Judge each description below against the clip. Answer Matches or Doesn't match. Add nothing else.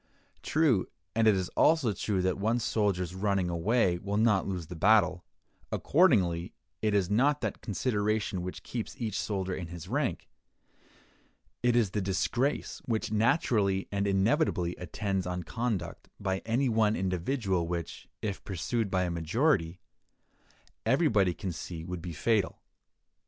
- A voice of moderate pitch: Doesn't match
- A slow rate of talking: Doesn't match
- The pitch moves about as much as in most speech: Matches